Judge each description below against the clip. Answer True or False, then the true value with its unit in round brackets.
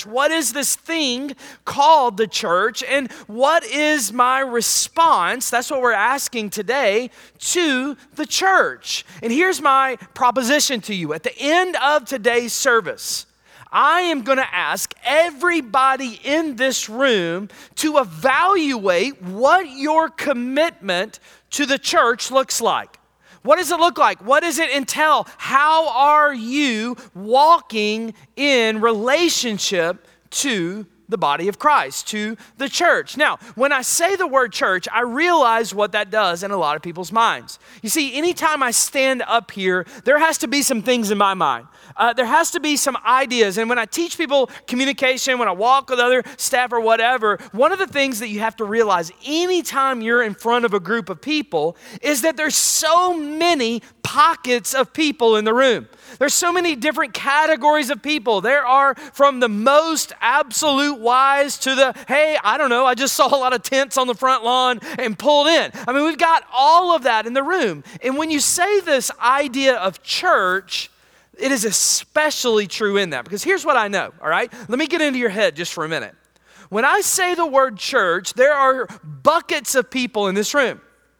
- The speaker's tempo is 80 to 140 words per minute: False (185 wpm)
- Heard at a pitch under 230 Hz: False (265 Hz)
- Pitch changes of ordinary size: True (4.6 semitones)